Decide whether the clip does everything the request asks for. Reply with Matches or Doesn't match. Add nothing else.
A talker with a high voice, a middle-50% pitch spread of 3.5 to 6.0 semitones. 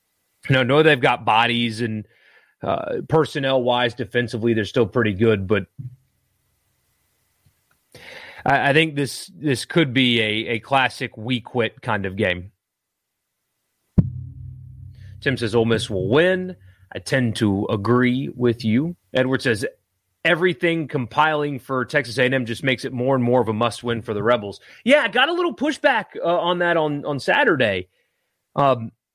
Doesn't match